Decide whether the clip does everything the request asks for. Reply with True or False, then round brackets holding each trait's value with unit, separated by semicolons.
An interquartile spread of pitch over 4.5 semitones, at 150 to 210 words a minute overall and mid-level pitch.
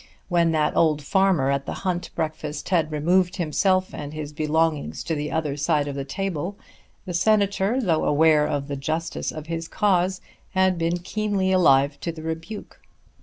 False (3.8 semitones; 170 wpm; 165 Hz)